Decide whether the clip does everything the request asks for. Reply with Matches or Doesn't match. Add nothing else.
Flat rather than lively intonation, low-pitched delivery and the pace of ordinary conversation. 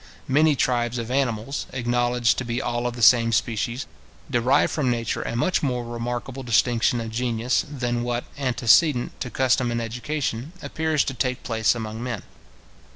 Matches